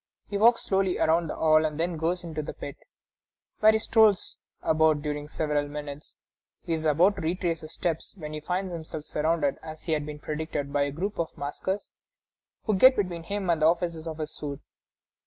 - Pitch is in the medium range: Yes, medium, 160 Hz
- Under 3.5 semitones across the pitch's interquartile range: Yes, average, 3.0 semitones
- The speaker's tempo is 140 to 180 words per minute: No, average, 195 wpm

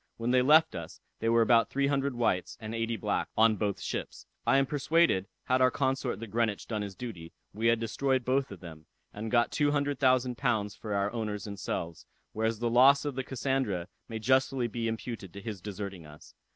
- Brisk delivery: Yes, fast, 210 wpm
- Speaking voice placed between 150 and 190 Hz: No, low, 115 Hz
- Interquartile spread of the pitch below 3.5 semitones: No, average, 4.0 semitones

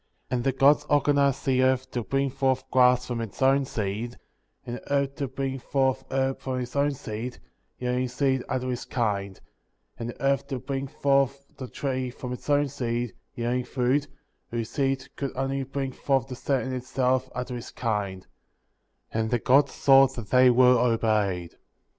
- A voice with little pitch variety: Yes, narrow, 2.0 semitones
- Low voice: Yes, low, 130 Hz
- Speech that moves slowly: No, average, 185 wpm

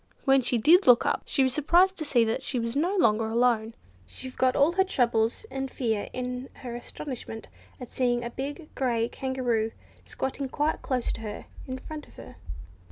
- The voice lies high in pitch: Yes, very high, 255 Hz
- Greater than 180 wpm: Yes, average, 190 wpm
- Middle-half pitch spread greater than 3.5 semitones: No, average, 3.1 semitones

